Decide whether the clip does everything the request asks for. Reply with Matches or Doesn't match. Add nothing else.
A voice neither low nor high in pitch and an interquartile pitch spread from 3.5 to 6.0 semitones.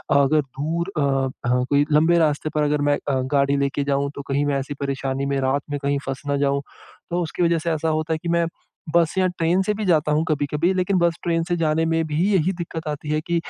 Doesn't match